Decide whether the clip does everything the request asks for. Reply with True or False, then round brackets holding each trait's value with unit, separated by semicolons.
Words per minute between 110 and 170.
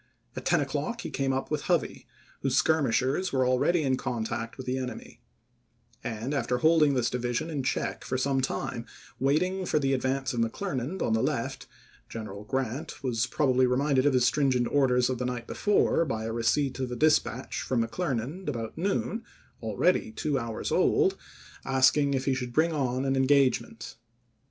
False (185 wpm)